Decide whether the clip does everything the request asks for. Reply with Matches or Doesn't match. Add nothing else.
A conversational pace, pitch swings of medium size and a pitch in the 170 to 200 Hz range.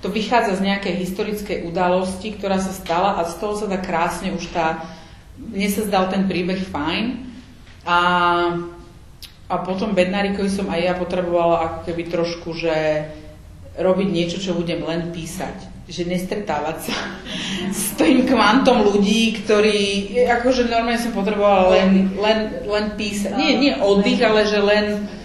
Matches